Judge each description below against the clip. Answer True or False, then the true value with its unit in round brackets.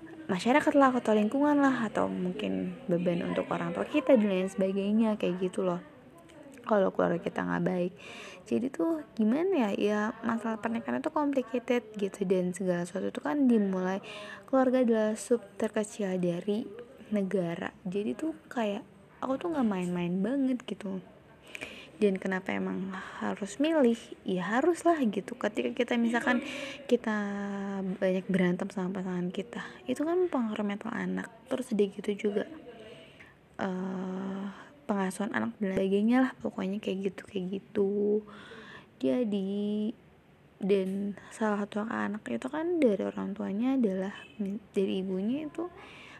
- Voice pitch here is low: False (205 Hz)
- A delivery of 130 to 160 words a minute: True (135 wpm)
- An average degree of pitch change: True (4.2 semitones)